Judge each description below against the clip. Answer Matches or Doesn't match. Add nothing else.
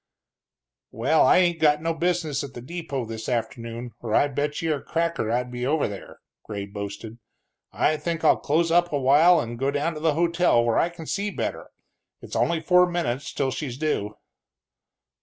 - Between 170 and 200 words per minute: Matches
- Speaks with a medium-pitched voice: Matches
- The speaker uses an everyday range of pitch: Doesn't match